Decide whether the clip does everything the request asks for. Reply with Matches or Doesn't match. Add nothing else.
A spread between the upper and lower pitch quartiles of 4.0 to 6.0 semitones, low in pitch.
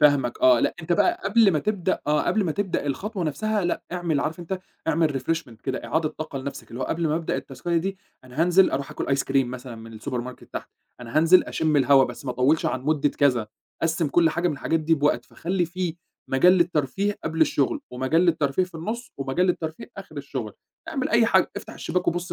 Doesn't match